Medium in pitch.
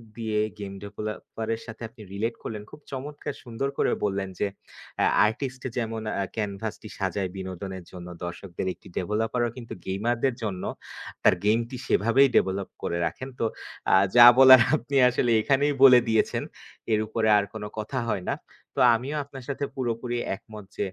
No: low, 110 Hz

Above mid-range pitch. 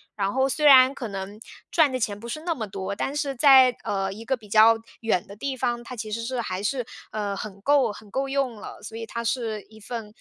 Yes: high, 230 Hz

